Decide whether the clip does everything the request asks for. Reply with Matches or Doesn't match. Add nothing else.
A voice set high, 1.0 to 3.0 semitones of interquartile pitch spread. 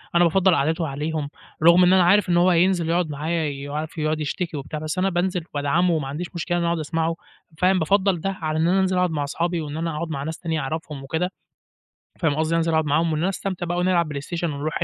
Doesn't match